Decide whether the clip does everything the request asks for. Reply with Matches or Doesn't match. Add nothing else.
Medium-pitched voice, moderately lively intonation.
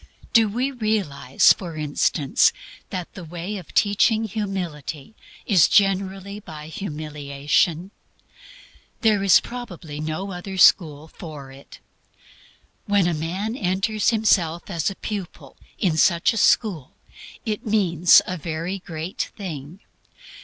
Matches